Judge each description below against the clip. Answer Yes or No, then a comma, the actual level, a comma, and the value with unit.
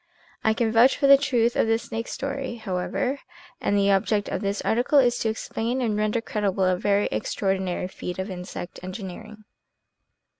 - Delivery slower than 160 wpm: No, average, 175 wpm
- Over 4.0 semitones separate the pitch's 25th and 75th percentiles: No, average, 3.7 semitones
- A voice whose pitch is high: Yes, high, 215 Hz